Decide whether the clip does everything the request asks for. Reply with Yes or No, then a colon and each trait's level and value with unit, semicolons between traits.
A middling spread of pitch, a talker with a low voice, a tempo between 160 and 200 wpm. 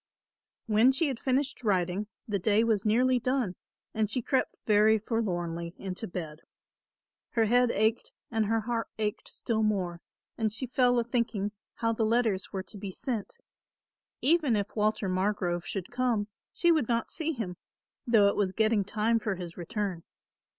No: average, 3.2 semitones; high, 220 Hz; average, 165 wpm